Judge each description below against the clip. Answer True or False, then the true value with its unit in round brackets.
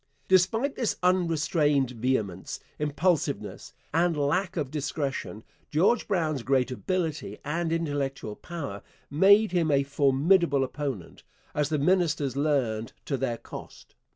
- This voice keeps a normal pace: False (120 wpm)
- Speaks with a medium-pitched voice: True (150 Hz)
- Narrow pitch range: False (4.2 semitones)